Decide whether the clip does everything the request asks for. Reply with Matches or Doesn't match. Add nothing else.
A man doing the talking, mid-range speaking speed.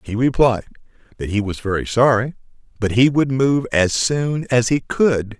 Matches